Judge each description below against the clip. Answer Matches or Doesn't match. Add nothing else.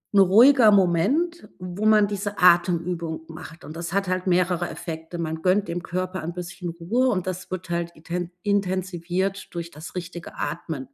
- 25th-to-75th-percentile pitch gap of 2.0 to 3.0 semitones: Matches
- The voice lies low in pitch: Doesn't match